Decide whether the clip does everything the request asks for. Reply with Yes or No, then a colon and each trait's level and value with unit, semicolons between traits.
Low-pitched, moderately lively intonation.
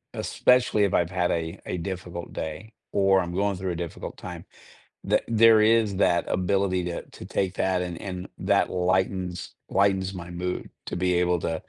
No: very low, 90 Hz; narrow, 1.9 semitones